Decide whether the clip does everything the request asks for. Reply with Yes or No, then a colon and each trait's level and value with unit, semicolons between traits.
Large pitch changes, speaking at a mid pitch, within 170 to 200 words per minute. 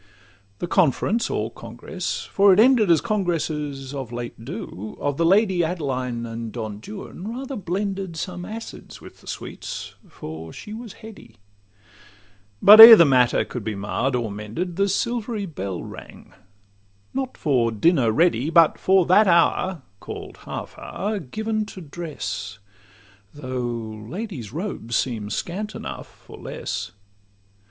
No: wide, 8.9 semitones; medium, 165 Hz; average, 140 wpm